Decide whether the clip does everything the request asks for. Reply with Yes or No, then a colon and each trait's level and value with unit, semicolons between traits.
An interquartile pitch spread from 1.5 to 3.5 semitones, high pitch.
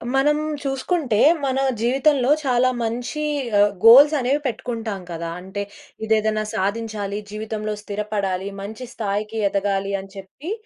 No: average, 4.1 semitones; high, 220 Hz